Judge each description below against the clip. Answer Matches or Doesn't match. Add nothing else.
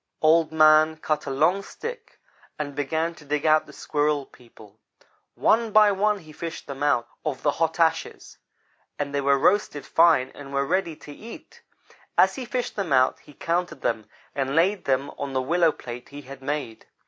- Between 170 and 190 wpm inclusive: Matches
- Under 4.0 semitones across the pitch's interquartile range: Matches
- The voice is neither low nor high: Matches